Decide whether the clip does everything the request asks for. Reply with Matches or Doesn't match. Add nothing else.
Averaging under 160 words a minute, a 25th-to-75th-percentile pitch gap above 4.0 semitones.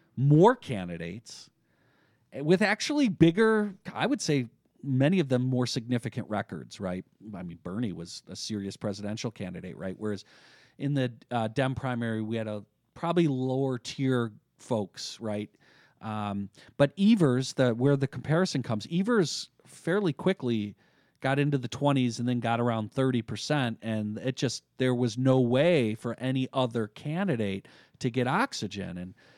Matches